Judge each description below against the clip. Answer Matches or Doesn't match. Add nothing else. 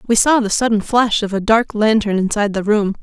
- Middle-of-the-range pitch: Doesn't match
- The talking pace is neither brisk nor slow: Doesn't match